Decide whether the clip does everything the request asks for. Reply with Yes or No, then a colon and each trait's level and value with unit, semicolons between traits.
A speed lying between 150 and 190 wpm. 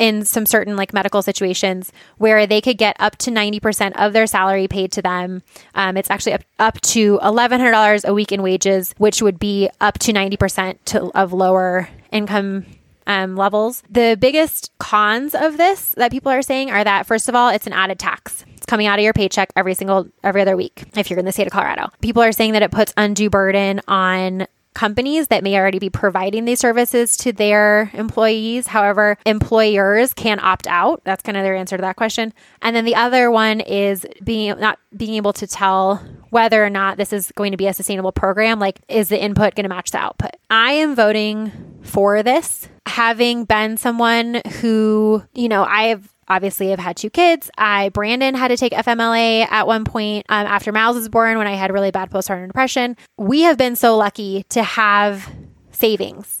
No: fast, 205 wpm